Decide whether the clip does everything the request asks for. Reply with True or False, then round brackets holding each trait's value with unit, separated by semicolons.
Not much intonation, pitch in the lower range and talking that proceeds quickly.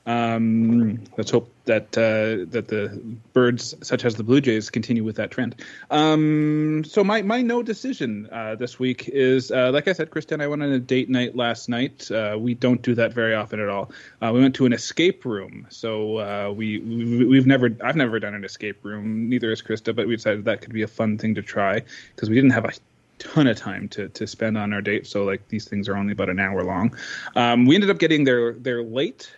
False (3.0 semitones; 115 Hz; 235 wpm)